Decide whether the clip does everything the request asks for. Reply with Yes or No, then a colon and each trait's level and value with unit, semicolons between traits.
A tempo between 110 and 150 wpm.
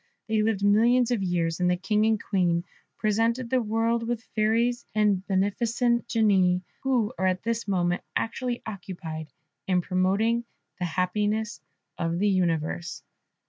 Yes: average, 140 wpm